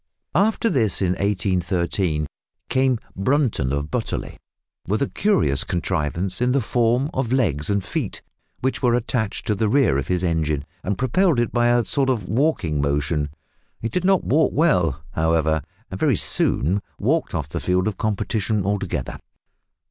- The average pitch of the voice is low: Yes, low, 100 Hz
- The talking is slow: No, average, 160 wpm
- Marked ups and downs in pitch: Yes, wide, 7.6 semitones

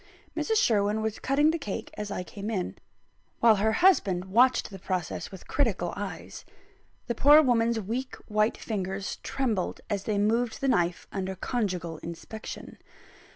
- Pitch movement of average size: Yes, average, 3.9 semitones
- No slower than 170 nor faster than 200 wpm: No, average, 155 wpm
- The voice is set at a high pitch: Yes, high, 210 Hz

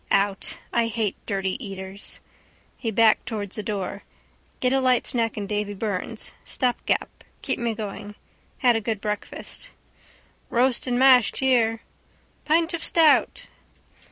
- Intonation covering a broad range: No, average, 3.6 semitones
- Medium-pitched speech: No, high, 225 Hz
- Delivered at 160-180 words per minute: No, slow, 135 wpm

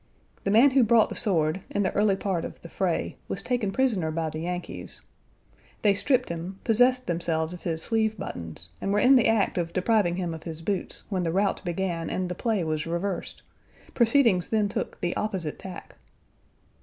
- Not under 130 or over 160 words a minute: No, average, 195 wpm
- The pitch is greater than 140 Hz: Yes, high, 190 Hz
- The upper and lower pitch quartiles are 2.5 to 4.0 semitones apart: No, average, 4.5 semitones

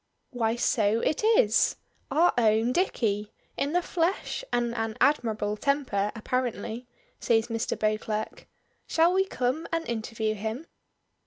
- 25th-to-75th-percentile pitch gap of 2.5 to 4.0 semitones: No, average, 5.3 semitones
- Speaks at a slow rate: Yes, slow, 130 wpm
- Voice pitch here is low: No, high, 235 Hz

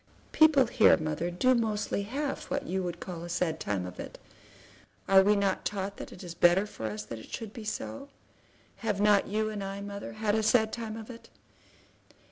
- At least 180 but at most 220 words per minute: Yes, average, 200 wpm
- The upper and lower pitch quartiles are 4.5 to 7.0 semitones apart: No, average, 3.8 semitones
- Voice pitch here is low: No, high, 200 Hz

